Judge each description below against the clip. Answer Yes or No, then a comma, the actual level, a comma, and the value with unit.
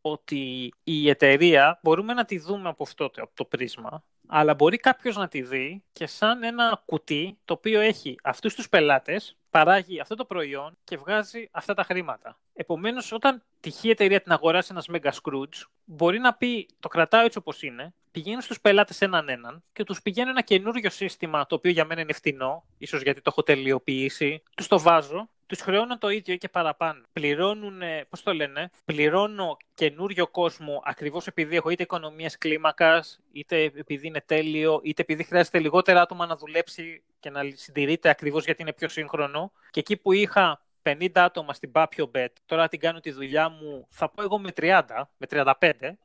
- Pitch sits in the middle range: Yes, medium, 165 Hz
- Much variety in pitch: No, average, 4.6 semitones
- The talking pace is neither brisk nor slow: No, fast, 180 wpm